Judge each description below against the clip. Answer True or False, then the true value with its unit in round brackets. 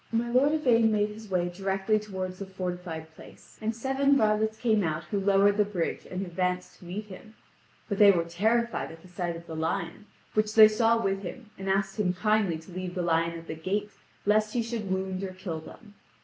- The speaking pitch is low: False (195 Hz)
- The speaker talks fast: True (210 wpm)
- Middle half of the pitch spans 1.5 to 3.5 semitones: True (3.2 semitones)